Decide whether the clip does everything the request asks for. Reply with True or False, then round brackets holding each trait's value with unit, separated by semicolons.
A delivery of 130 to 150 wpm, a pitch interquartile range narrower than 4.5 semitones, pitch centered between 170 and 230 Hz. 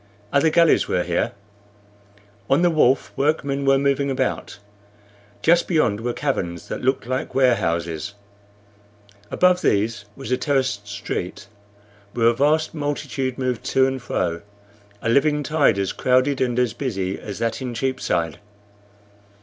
False (140 wpm; 3.8 semitones; 130 Hz)